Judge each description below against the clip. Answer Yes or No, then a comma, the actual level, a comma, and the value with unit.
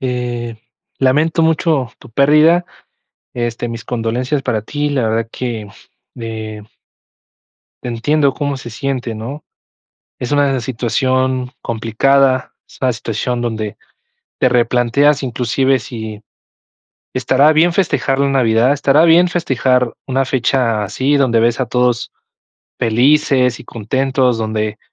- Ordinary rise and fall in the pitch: Yes, average, 3.0 semitones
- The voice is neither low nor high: No, low, 125 Hz